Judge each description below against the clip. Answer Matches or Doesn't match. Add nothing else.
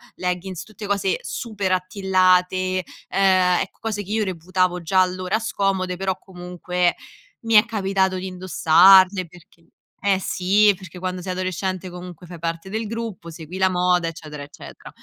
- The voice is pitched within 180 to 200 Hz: Matches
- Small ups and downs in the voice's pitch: Matches